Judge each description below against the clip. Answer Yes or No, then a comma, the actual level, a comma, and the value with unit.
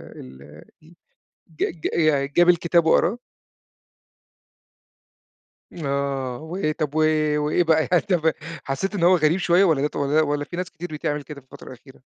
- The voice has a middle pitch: Yes, medium, 155 Hz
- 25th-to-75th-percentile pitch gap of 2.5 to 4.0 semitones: Yes, average, 3.6 semitones